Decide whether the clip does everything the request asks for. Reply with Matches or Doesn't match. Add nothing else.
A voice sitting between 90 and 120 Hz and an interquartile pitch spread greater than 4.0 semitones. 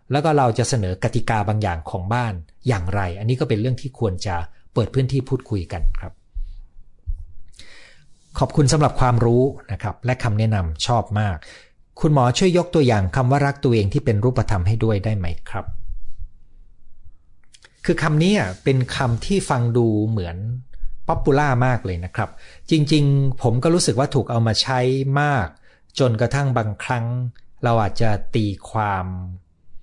Matches